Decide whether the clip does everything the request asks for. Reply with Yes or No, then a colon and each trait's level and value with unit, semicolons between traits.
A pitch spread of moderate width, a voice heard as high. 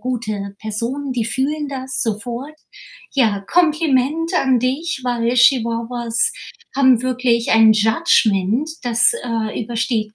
Yes: average, 3.2 semitones; high, 245 Hz